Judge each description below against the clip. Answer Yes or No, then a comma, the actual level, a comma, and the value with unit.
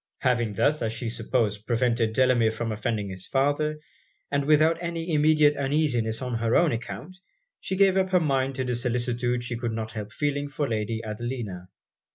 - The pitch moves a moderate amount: Yes, average, 4.5 semitones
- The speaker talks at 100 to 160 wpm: No, average, 180 wpm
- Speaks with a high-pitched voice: No, low, 125 Hz